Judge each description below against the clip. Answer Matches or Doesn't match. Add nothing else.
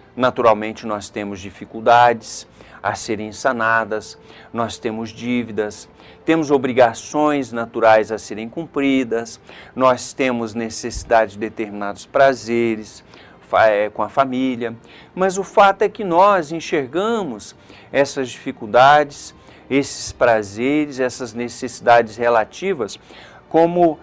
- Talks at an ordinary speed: Doesn't match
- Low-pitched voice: Matches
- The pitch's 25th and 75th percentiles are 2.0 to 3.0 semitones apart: Doesn't match